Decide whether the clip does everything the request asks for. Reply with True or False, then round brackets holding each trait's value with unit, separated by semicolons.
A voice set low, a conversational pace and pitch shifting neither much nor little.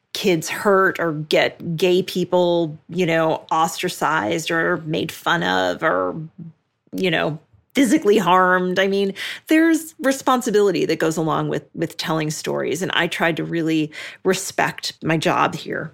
False (170 Hz; 145 wpm; 3.1 semitones)